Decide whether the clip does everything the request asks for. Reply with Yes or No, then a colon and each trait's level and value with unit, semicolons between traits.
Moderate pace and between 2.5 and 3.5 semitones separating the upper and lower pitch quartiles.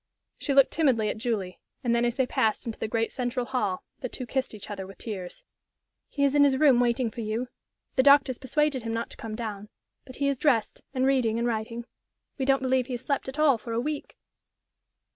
No: fast, 225 wpm; average, 3.1 semitones